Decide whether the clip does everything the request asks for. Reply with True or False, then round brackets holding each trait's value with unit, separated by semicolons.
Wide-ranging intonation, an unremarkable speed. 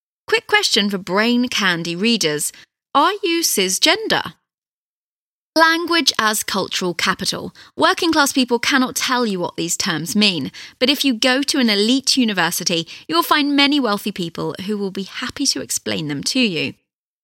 True (7.0 semitones; 155 wpm)